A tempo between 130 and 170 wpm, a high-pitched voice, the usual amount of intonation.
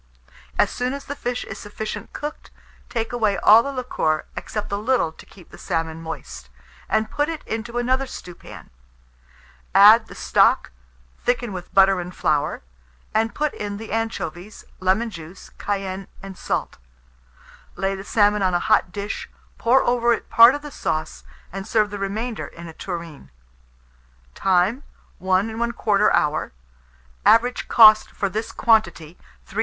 Yes: average, 155 wpm; high, 210 Hz; average, 4.0 semitones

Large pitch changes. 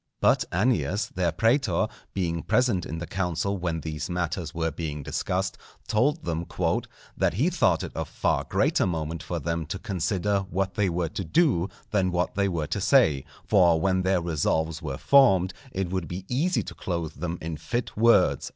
No: average, 3.2 semitones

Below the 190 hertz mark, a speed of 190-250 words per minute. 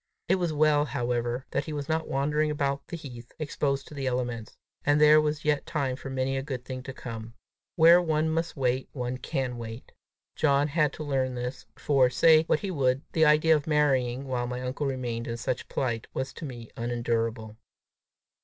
Yes: low, 135 Hz; average, 195 wpm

